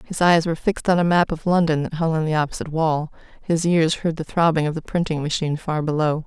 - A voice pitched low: No, medium, 160 Hz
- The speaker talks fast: Yes, fast, 250 wpm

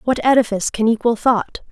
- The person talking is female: Yes, female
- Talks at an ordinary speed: Yes, average, 175 wpm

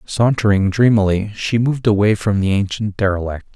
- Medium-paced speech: Yes, average, 150 wpm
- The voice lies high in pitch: No, low, 105 Hz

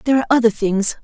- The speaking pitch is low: No, high, 230 Hz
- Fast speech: Yes, fast, 230 wpm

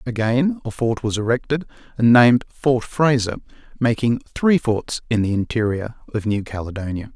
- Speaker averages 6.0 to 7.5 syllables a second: No, 5.1 syllables/s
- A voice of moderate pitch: No, low, 115 Hz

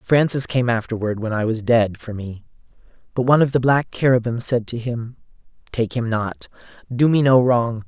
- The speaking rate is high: No, average, 190 wpm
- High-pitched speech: No, low, 120 Hz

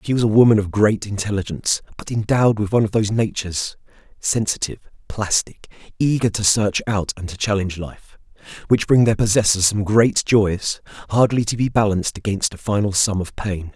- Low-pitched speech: Yes, low, 105 Hz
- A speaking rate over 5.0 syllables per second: Yes, 5.7 syllables/s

